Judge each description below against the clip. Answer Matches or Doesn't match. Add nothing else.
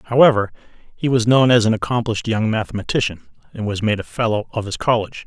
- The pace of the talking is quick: Doesn't match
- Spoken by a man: Matches